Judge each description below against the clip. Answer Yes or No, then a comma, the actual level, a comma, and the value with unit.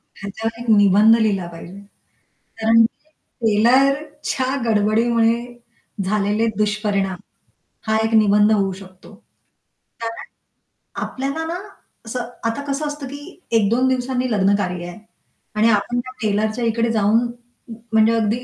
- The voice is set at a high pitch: Yes, high, 220 Hz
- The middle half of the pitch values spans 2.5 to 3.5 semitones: Yes, average, 2.9 semitones